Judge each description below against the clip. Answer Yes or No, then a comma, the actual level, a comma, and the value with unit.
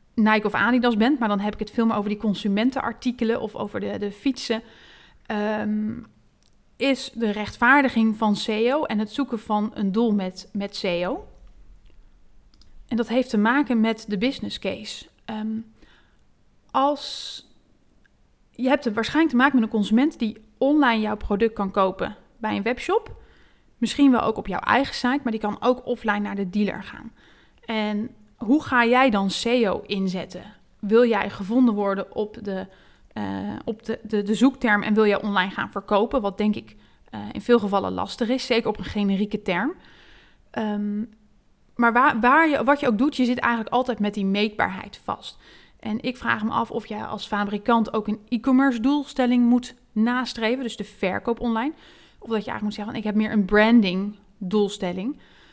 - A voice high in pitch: Yes, high, 220 Hz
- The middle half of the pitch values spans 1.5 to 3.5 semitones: Yes, average, 2.8 semitones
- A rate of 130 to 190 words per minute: Yes, average, 180 wpm